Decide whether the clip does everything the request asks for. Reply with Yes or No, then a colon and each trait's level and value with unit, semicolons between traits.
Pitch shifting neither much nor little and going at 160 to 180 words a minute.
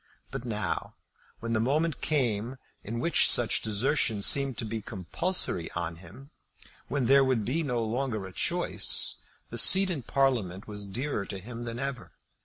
Yes: average, 4.7 semitones; average, 165 wpm